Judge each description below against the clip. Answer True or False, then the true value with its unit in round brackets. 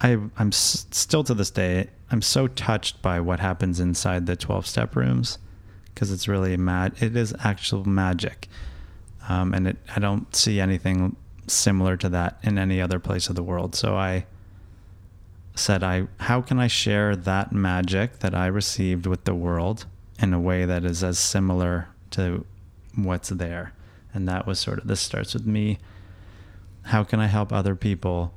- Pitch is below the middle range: True (95 Hz)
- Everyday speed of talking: True (175 wpm)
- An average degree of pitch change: False (2.2 semitones)